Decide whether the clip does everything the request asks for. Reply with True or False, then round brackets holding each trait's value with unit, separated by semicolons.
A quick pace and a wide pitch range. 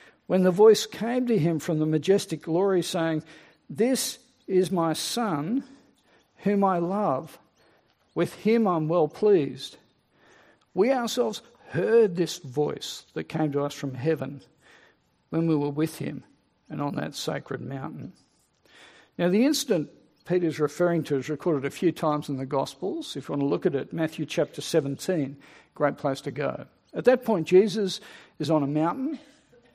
False (160 wpm; 5.8 semitones)